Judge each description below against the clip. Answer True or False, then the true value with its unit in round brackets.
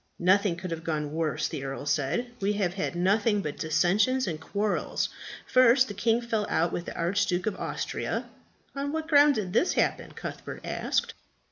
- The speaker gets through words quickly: False (175 wpm)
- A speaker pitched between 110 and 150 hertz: False (195 Hz)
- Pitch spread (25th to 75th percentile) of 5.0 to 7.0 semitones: True (5.4 semitones)